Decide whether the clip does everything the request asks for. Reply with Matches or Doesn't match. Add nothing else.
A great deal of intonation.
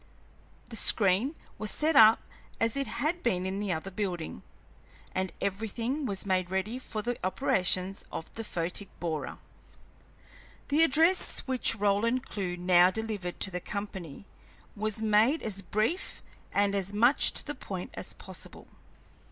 Doesn't match